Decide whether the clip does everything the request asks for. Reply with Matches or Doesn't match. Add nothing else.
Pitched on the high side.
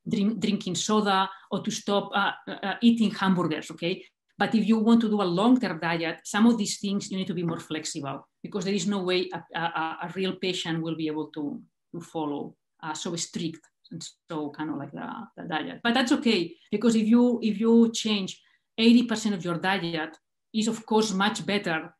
Matches